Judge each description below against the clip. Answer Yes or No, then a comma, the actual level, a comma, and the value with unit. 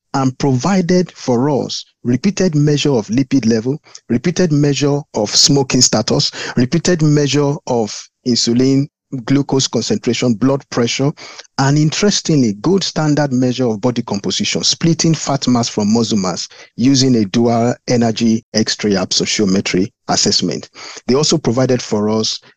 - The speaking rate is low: Yes, slow, 130 wpm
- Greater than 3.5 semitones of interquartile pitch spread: Yes, average, 3.9 semitones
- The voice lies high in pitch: No, low, 135 Hz